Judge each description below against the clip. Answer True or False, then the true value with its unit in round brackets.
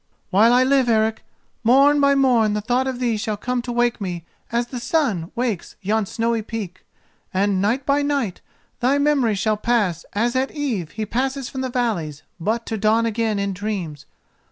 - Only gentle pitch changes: False (3.7 semitones)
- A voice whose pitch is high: True (230 Hz)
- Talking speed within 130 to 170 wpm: False (185 wpm)